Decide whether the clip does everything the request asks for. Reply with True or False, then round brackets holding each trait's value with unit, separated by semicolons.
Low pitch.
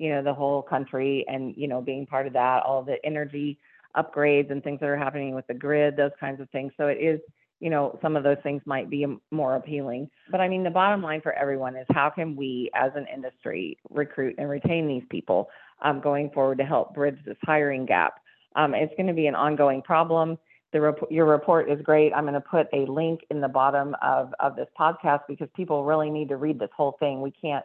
False (145 Hz)